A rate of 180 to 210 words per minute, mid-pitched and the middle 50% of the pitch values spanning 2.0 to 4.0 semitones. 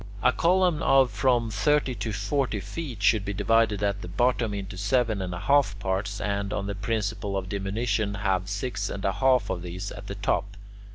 No: average, 195 wpm; low, 105 Hz; average, 3.4 semitones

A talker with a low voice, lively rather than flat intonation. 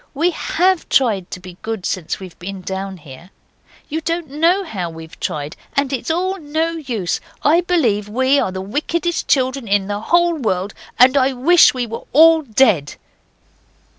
No: very high, 255 Hz; wide, 9.0 semitones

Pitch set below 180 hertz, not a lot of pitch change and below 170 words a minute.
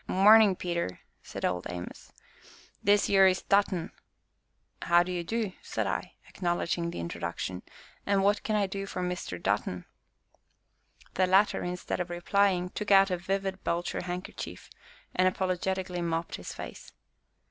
No: medium, 185 Hz; narrow, 2.3 semitones; average, 145 wpm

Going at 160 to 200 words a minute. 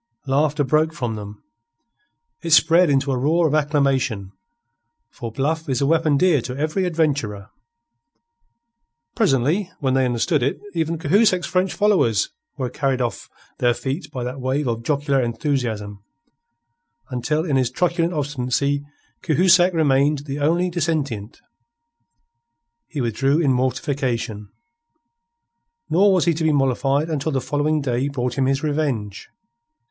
No: slow, 135 wpm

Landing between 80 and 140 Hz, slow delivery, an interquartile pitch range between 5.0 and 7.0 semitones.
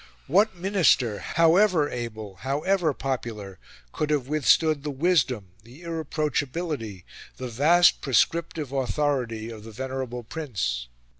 Yes: low, 135 Hz; slow, 115 wpm; wide, 5.6 semitones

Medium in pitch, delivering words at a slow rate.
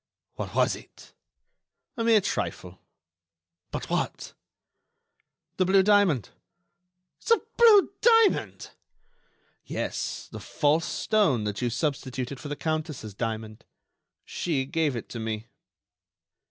Yes: medium, 145 Hz; slow, 110 wpm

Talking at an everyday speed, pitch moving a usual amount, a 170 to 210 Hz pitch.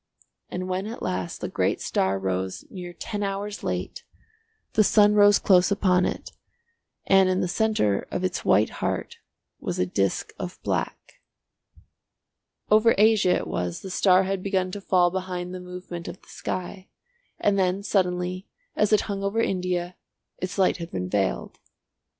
No: average, 160 wpm; narrow, 2.0 semitones; medium, 185 Hz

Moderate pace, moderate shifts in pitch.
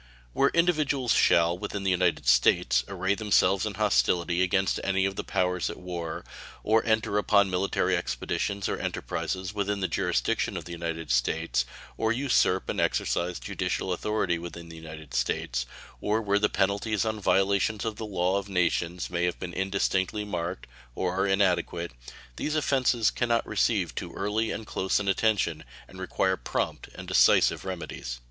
Yes: average, 165 wpm; average, 3.2 semitones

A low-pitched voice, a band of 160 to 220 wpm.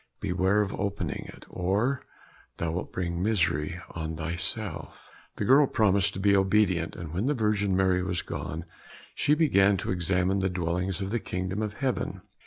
Yes: very low, 95 Hz; average, 170 wpm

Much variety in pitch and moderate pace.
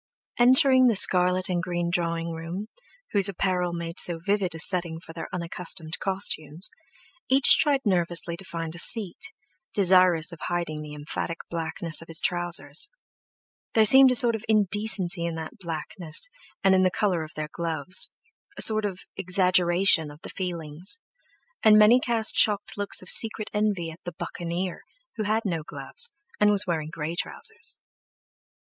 No: average, 3.8 semitones; average, 160 wpm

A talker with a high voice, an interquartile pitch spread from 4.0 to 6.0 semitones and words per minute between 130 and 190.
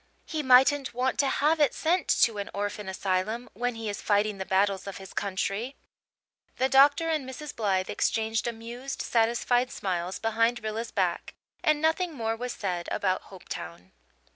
Yes: high, 225 Hz; average, 4.8 semitones; average, 165 wpm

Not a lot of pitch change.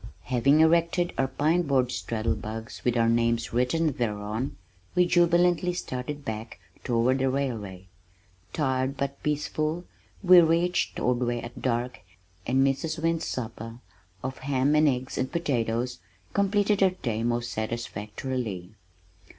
No: average, 5.2 semitones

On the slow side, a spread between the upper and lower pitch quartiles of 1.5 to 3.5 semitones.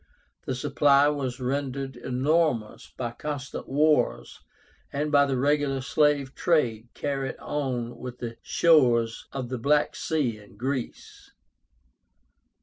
Yes: slow, 120 wpm; average, 2.9 semitones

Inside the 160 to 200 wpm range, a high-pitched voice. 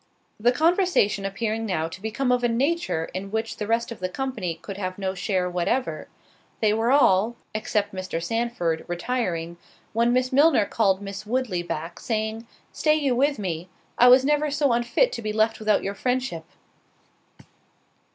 Yes: average, 170 wpm; high, 220 Hz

